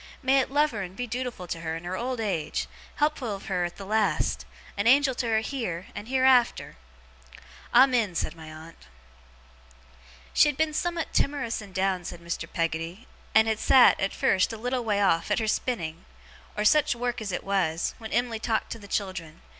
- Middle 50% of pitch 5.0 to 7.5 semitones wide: Yes, wide, 5.6 semitones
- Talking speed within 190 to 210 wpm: Yes, average, 195 wpm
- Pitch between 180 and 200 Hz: No, high, 220 Hz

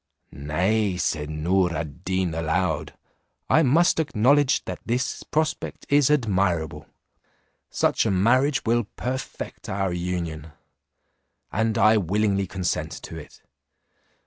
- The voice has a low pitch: Yes, very low, 95 Hz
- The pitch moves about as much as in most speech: No, wide, 6.2 semitones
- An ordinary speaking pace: No, slow, 115 wpm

